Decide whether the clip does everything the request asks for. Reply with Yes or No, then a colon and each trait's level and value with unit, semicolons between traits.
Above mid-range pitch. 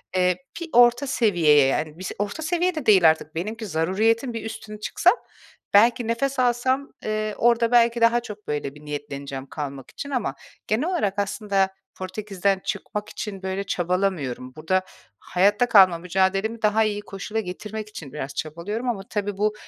Yes: high, 205 Hz